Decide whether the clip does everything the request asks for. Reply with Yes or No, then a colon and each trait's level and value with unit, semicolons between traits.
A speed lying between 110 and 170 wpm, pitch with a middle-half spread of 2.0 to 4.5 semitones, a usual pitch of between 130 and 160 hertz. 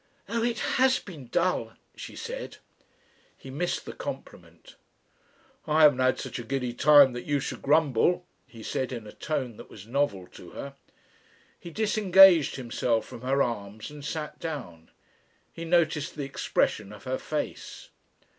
No: average, 155 wpm; wide, 5.4 semitones; medium, 140 Hz